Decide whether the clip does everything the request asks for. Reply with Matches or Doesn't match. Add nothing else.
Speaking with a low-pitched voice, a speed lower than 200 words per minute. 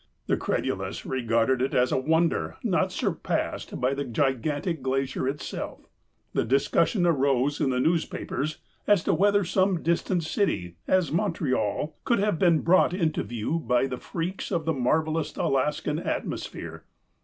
Doesn't match